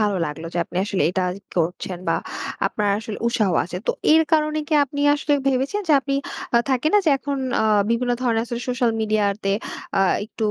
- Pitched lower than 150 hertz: No, high, 230 Hz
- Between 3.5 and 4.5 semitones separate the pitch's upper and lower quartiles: No, wide, 5.5 semitones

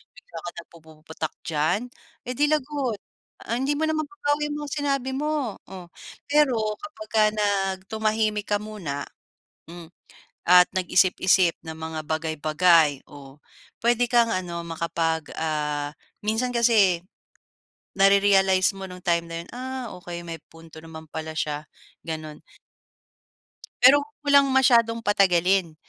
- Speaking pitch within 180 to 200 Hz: Yes, high, 190 Hz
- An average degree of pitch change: No, wide, 6.6 semitones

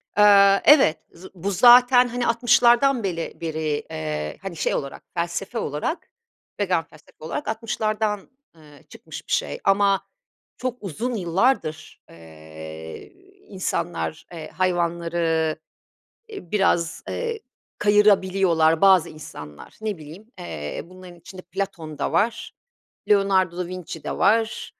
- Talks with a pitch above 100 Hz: Yes, medium, 185 Hz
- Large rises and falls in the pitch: No, average, 4.6 semitones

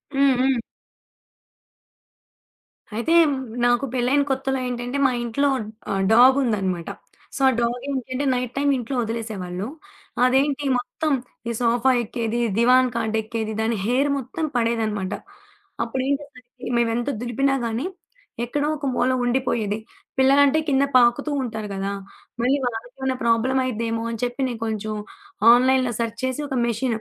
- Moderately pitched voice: No, high, 245 Hz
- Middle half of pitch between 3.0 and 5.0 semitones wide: No, narrow, 2.6 semitones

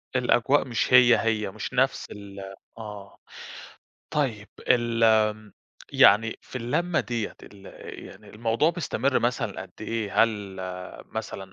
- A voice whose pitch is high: No, low, 115 Hz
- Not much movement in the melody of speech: No, average, 3.0 semitones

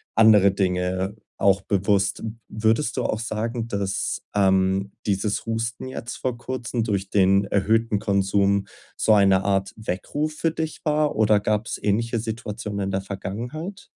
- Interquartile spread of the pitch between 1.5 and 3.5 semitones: Yes, average, 2.8 semitones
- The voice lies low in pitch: Yes, low, 105 Hz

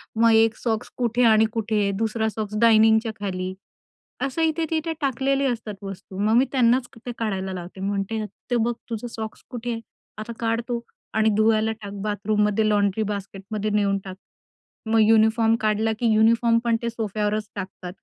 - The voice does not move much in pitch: Yes, narrow, 2.0 semitones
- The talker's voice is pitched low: No, high, 220 Hz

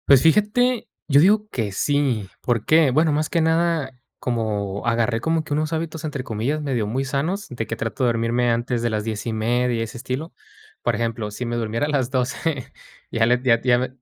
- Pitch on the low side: Yes, low, 125 Hz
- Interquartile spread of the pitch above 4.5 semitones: Yes, average, 4.9 semitones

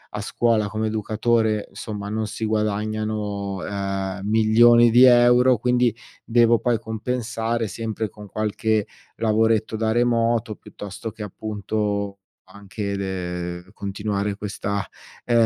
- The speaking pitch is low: Yes, low, 110 Hz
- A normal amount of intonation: No, narrow, 2.1 semitones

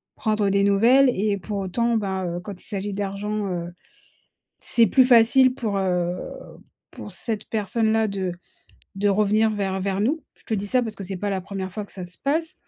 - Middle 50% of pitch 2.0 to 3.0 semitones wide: Yes, narrow, 2.5 semitones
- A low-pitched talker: No, high, 205 Hz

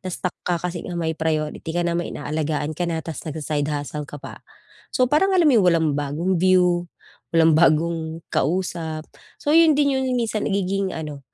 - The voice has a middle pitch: Yes, medium, 170 Hz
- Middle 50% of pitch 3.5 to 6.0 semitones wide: No, average, 3.1 semitones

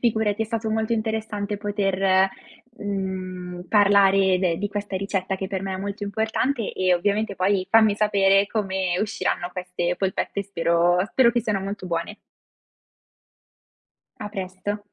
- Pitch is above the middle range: Yes, high, 200 Hz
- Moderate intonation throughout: No, narrow, 2.0 semitones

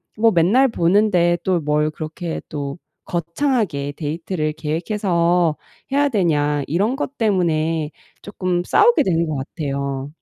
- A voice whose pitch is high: No, medium, 170 Hz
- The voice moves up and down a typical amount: Yes, average, 4.7 semitones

